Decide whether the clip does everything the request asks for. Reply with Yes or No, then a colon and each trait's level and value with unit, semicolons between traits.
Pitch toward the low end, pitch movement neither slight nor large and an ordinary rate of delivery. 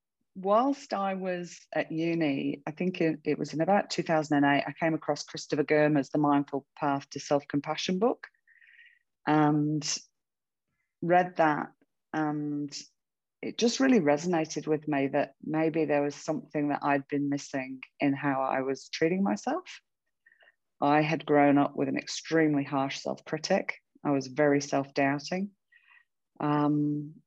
No: medium, 150 Hz; average, 3.8 semitones; average, 145 wpm